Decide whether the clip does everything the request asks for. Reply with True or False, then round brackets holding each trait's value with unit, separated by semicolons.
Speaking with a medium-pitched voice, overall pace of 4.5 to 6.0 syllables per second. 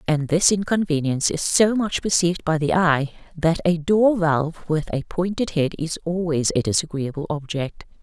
True (165 Hz; 4.9 syllables/s)